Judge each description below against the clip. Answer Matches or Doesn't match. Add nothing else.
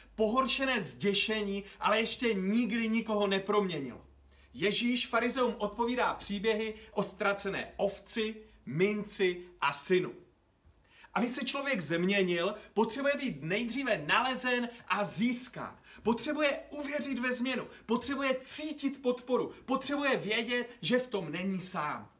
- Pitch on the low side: Doesn't match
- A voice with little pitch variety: Doesn't match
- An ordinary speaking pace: Doesn't match